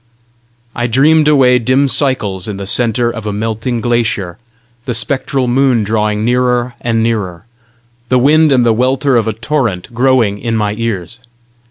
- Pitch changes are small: No, average, 3.1 semitones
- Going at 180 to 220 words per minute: No, average, 160 wpm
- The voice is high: No, low, 120 Hz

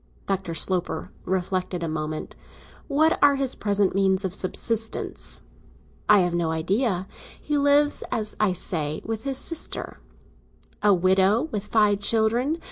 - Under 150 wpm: Yes, slow, 135 wpm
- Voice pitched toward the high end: Yes, high, 200 Hz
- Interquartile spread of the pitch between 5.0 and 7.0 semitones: No, average, 4.1 semitones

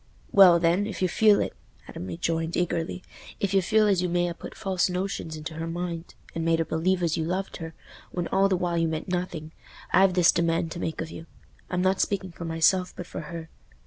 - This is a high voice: No, medium, 175 Hz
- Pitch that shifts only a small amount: Yes, narrow, 2.2 semitones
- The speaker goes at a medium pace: No, fast, 220 wpm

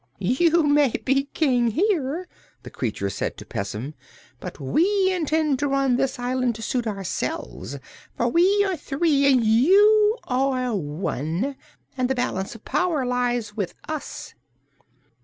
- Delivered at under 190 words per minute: Yes, average, 140 wpm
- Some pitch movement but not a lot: No, wide, 5.8 semitones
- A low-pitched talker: No, very high, 265 Hz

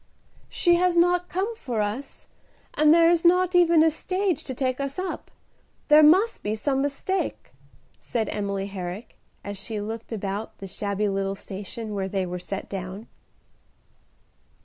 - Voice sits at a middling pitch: No, high, 240 Hz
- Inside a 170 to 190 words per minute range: No, average, 155 wpm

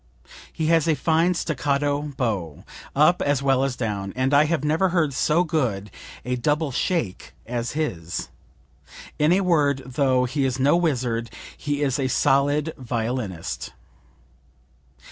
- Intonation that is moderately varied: Yes, average, 3.8 semitones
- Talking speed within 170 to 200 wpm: No, average, 145 wpm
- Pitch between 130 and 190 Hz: Yes, medium, 140 Hz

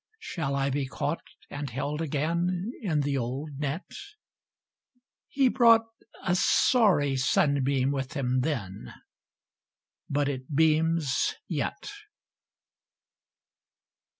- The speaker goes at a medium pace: No, slow, 100 wpm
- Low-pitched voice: No, medium, 145 Hz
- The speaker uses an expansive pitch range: No, average, 3.6 semitones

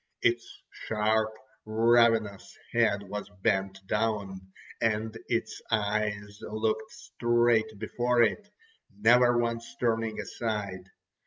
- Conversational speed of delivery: No, slow, 95 wpm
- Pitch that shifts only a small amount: Yes, narrow, 2.2 semitones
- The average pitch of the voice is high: No, low, 110 Hz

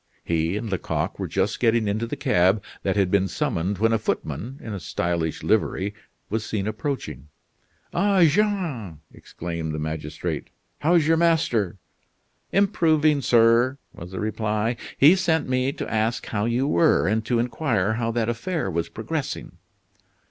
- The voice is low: Yes, low, 110 Hz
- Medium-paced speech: Yes, average, 155 wpm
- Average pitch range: No, wide, 6.4 semitones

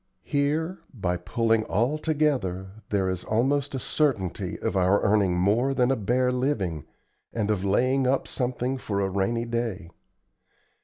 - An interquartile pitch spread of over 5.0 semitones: Yes, wide, 5.5 semitones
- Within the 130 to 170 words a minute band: Yes, average, 150 wpm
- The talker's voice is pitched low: Yes, low, 115 Hz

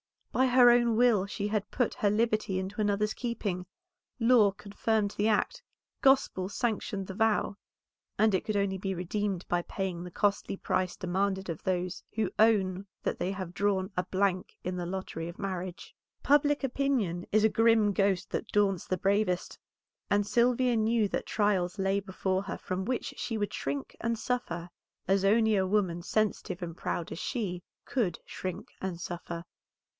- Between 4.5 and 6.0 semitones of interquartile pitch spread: No, average, 2.9 semitones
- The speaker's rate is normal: Yes, average, 170 wpm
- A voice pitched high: Yes, high, 200 Hz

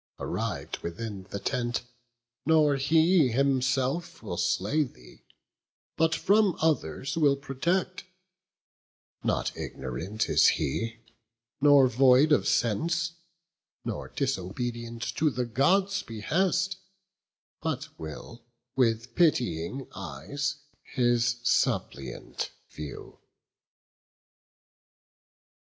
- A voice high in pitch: No, low, 130 Hz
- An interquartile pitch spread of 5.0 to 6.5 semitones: Yes, wide, 5.6 semitones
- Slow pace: Yes, slow, 85 wpm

